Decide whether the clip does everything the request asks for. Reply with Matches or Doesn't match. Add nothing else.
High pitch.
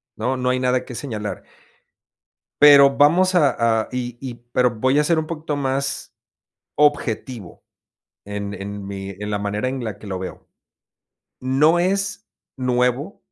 Doesn't match